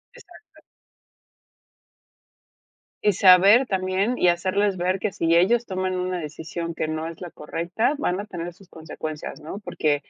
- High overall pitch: No, medium, 180 Hz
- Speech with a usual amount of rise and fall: Yes, average, 3.1 semitones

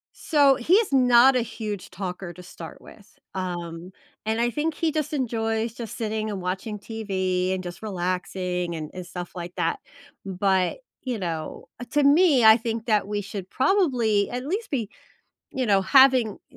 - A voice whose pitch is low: No, high, 215 Hz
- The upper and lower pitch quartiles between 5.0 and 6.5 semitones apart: Yes, wide, 5.4 semitones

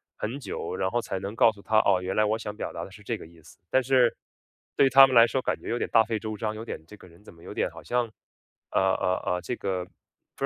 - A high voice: No, low, 110 Hz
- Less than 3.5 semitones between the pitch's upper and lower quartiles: No, average, 3.9 semitones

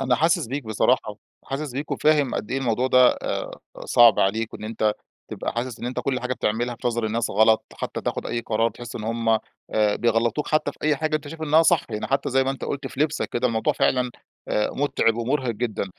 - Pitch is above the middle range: No, low, 120 Hz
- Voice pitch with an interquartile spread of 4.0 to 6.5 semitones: No, average, 3.3 semitones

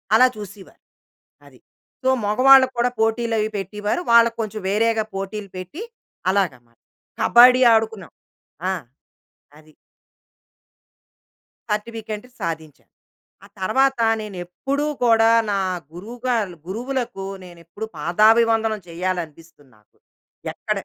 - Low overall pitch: No, high, 215 Hz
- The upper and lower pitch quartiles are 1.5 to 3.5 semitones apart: No, average, 4.1 semitones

